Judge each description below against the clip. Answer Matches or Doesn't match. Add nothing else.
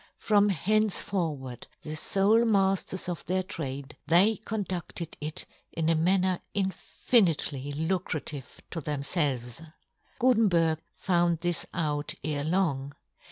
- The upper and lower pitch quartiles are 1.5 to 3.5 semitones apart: Doesn't match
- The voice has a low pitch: Doesn't match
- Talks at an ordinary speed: Doesn't match